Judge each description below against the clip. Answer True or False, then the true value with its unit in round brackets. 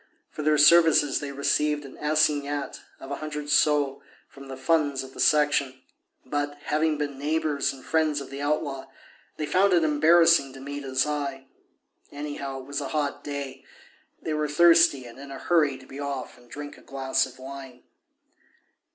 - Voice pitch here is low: False (145 Hz)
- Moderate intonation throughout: False (1.8 semitones)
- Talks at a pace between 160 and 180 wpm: True (175 wpm)